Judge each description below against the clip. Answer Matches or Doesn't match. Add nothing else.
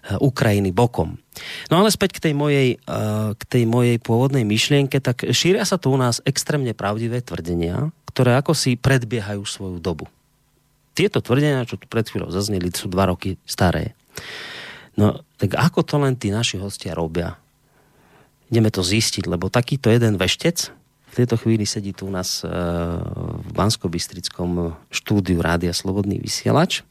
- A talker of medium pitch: Doesn't match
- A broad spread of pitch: Matches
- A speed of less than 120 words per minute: Doesn't match